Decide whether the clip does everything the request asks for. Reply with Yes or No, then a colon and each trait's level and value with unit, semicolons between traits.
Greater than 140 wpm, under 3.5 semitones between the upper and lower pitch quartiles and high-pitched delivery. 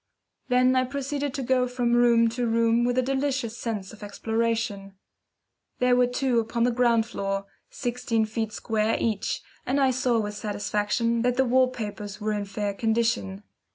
Yes: average, 170 wpm; average, 2.7 semitones; high, 230 Hz